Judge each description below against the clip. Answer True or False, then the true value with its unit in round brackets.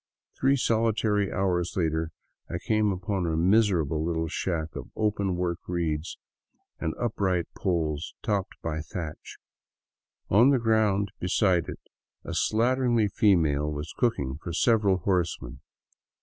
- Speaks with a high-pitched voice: False (90 Hz)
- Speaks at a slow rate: True (125 wpm)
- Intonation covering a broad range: False (4.7 semitones)